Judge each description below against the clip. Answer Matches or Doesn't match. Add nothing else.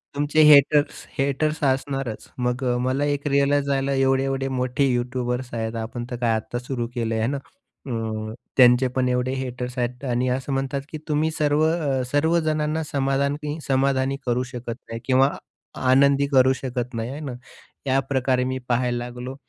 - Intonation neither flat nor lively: Doesn't match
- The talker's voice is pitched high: Doesn't match